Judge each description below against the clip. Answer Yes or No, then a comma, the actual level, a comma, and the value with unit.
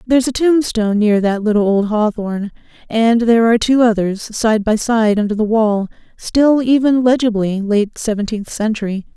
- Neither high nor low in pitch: No, high, 220 Hz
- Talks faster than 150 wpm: Yes, average, 165 wpm